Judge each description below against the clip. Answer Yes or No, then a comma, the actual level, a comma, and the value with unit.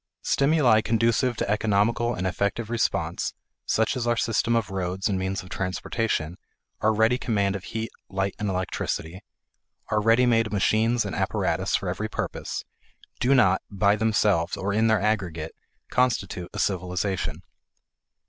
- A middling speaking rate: Yes, average, 150 wpm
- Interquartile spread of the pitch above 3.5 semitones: No, average, 3.2 semitones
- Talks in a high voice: No, low, 105 Hz